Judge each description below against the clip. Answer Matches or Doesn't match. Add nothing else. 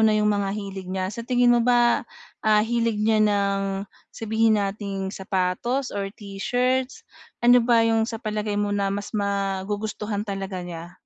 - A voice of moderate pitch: Doesn't match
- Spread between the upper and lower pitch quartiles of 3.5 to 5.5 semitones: Doesn't match